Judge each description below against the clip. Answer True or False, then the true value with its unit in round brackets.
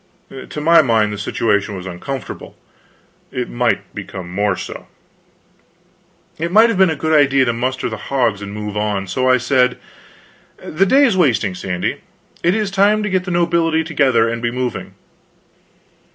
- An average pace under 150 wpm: False (165 wpm)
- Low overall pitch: True (130 Hz)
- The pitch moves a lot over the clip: True (8.1 semitones)